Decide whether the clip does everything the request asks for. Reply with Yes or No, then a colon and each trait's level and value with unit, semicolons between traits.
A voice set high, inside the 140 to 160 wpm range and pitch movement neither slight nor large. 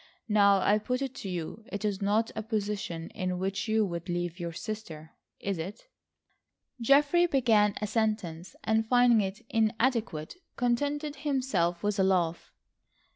Yes: high, 210 Hz; average, 150 wpm; average, 4.2 semitones